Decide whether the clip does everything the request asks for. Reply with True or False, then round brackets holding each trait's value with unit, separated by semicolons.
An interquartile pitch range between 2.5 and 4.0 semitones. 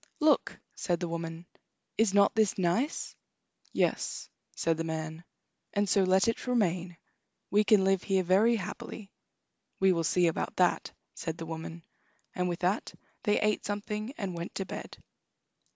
True (3.6 semitones)